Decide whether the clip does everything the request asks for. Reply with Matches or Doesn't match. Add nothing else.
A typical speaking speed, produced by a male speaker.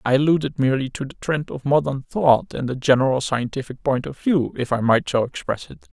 Doesn't match